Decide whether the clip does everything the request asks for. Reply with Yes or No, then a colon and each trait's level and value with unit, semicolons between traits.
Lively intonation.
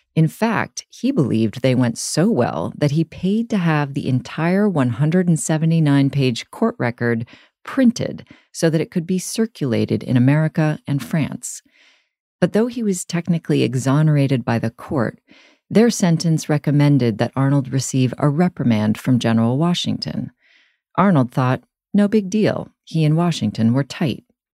Yes: wide, 5.9 semitones